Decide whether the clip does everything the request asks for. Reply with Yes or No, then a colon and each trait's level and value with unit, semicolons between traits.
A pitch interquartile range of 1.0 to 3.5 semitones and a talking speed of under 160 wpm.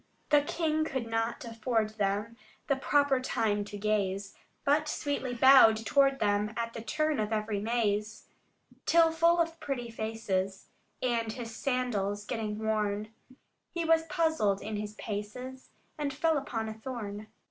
No: average, 4.5 semitones; average, 145 wpm